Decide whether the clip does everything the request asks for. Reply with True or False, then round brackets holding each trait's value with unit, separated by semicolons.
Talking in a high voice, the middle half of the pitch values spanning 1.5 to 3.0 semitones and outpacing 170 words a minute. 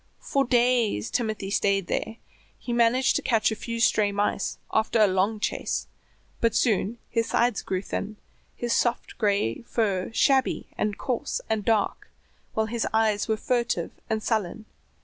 False (220 Hz; 2.5 semitones; 155 wpm)